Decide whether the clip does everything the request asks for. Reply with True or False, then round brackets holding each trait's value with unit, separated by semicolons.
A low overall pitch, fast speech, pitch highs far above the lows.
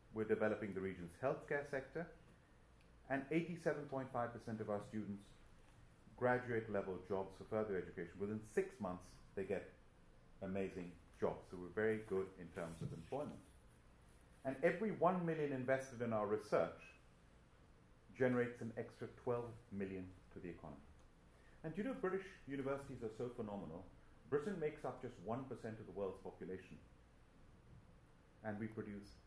False (110 Hz; 140 wpm; 5.7 semitones)